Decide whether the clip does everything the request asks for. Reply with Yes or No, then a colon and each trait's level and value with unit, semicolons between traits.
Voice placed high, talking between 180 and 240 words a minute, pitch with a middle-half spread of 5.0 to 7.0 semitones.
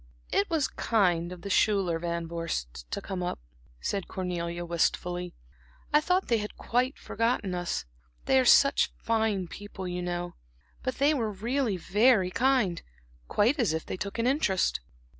No: high, 195 Hz; average, 160 wpm; average, 5.3 semitones